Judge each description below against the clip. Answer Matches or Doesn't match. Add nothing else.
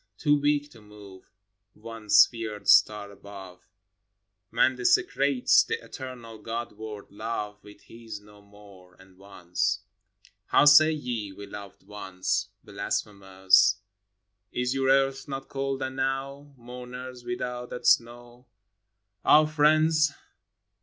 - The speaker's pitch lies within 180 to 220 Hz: Doesn't match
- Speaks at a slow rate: Matches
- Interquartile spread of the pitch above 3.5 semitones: Matches